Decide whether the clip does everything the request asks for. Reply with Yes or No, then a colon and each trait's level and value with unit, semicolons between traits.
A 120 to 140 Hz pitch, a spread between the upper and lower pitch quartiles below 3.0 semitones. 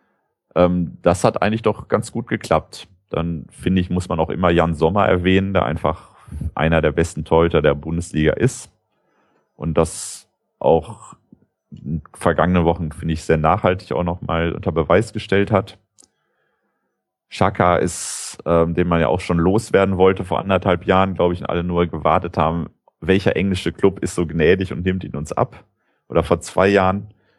No: very low, 90 Hz; narrow, 2.5 semitones